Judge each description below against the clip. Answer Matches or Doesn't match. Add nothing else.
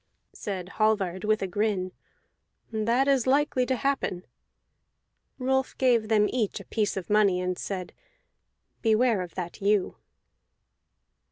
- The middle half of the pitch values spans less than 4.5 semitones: Doesn't match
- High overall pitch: Matches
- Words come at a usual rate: Doesn't match